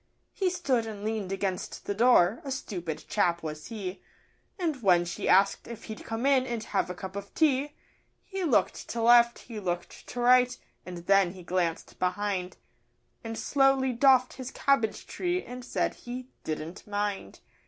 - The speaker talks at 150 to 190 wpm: Yes, average, 170 wpm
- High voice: Yes, high, 220 Hz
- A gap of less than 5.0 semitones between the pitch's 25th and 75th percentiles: No, wide, 5.5 semitones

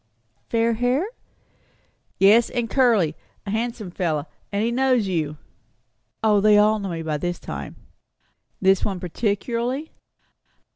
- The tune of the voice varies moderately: Yes, average, 4.5 semitones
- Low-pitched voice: No, high, 210 Hz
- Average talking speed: No, slow, 130 wpm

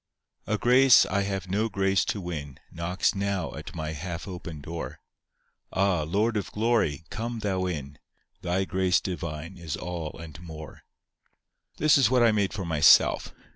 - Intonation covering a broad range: No, average, 3.9 semitones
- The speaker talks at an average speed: Yes, average, 160 wpm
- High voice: No, very low, 90 Hz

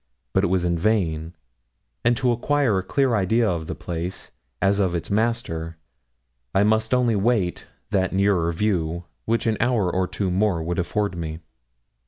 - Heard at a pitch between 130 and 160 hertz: No, very low, 95 Hz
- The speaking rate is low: No, average, 165 wpm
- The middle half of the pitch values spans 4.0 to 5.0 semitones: Yes, average, 4.4 semitones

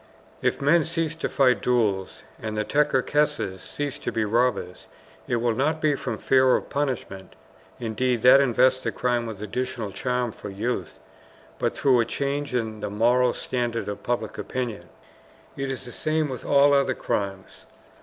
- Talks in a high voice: No, low, 125 Hz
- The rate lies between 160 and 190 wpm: Yes, average, 165 wpm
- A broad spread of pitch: No, average, 3.9 semitones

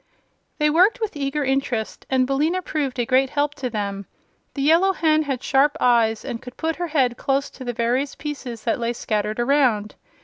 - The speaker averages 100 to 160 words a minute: No, average, 195 wpm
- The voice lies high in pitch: Yes, very high, 270 Hz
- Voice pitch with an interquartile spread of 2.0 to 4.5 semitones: Yes, average, 3.8 semitones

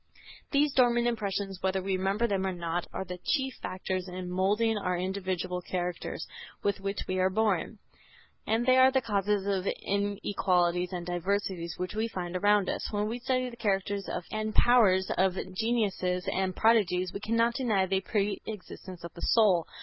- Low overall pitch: No, high, 195 Hz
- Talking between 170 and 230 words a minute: Yes, average, 175 wpm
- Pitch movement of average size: Yes, average, 3.1 semitones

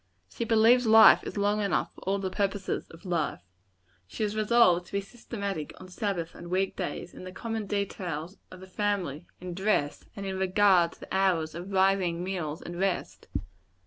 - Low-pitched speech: No, high, 190 Hz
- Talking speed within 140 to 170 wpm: No, average, 190 wpm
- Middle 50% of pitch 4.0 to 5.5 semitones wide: No, average, 2.8 semitones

